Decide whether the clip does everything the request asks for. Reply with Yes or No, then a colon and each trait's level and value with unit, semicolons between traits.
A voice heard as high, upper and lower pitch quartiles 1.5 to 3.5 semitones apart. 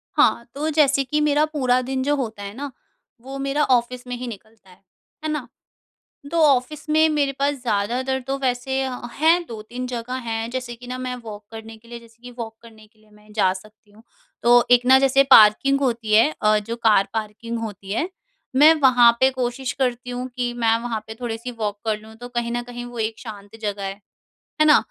Yes: high, 240 Hz; average, 3.1 semitones